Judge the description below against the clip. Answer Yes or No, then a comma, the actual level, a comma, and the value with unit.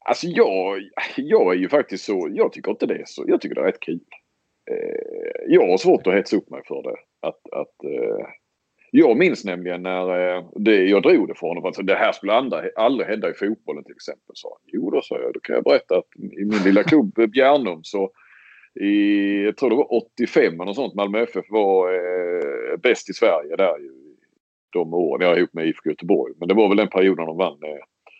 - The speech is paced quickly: Yes, fast, 200 wpm